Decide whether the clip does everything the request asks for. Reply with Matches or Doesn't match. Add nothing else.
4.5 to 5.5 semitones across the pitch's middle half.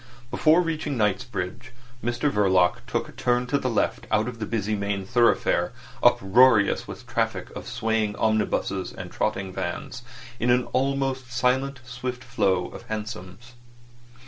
Doesn't match